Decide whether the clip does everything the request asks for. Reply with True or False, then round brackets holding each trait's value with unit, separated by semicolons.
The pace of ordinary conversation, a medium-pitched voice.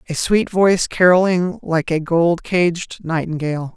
True (145 wpm; 170 Hz)